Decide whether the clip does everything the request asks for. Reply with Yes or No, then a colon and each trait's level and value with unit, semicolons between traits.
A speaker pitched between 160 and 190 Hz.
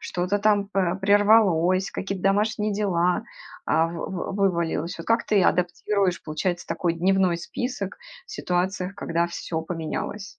Yes: medium, 185 Hz